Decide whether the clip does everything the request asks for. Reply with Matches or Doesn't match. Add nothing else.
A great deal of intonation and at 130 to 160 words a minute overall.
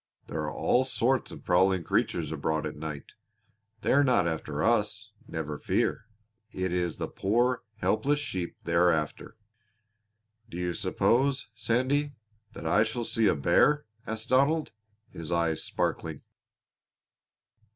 Matches